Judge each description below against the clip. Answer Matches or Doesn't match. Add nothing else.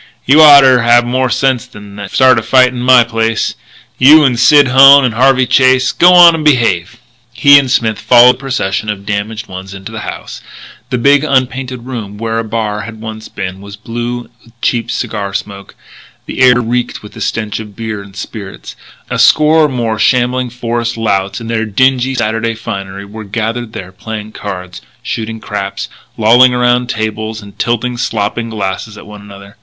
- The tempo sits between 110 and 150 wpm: Doesn't match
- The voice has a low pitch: Matches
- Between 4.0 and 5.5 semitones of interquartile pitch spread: Doesn't match